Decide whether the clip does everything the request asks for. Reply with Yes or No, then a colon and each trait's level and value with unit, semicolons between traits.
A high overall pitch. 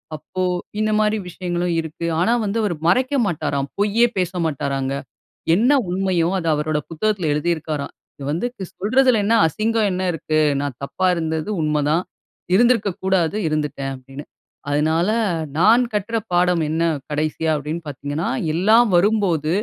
No: medium, 175 Hz